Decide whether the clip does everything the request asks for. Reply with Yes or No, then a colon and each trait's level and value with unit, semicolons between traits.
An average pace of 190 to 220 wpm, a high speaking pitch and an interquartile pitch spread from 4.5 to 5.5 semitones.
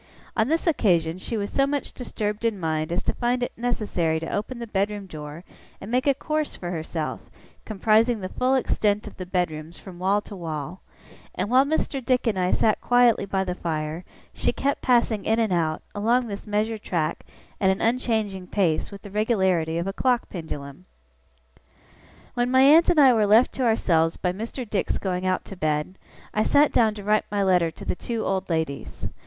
Yes: average, 200 wpm; high, 205 Hz; average, 5.0 semitones